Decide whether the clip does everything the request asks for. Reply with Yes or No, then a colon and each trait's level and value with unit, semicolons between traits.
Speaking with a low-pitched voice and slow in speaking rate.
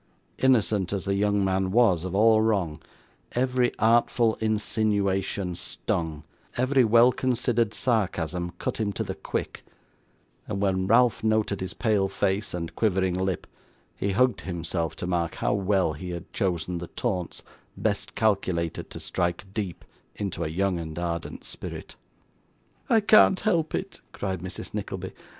No: low, 100 Hz; average, 145 wpm